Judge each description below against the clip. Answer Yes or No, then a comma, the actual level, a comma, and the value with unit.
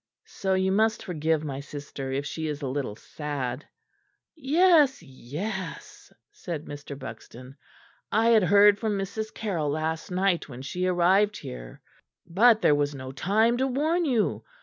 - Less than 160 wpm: Yes, average, 150 wpm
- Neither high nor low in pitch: Yes, medium, 175 Hz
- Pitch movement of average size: No, wide, 7.1 semitones